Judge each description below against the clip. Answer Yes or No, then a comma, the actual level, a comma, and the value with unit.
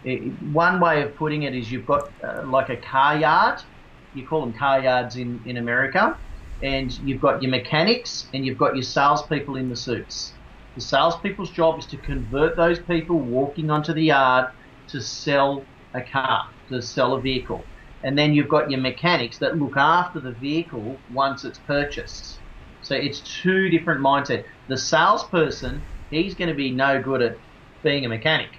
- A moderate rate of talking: Yes, average, 180 wpm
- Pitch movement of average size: Yes, average, 3.2 semitones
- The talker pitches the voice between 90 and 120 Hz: No, low, 135 Hz